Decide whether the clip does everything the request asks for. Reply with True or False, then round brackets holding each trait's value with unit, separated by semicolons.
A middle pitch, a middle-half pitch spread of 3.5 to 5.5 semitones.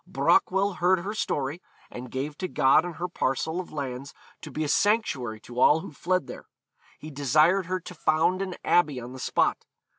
True (155 Hz; 5.1 semitones)